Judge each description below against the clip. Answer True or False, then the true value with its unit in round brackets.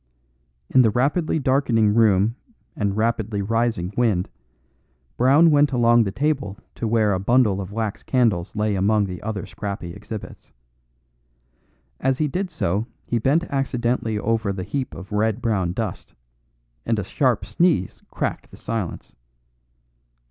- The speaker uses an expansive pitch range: False (4.0 semitones)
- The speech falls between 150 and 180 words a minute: False (140 wpm)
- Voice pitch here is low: True (110 Hz)